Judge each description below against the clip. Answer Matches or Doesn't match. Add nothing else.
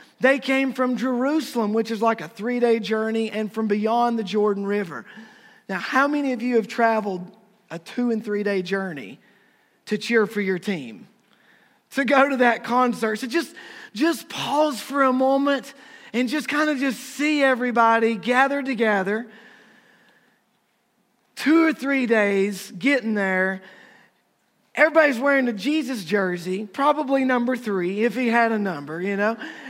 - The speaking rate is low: Doesn't match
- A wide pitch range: Doesn't match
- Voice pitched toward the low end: Doesn't match